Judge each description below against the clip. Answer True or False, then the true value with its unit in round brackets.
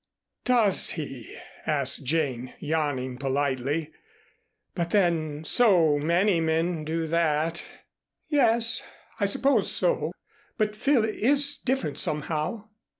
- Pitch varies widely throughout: True (6.3 semitones)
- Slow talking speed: True (100 wpm)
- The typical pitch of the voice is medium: True (165 Hz)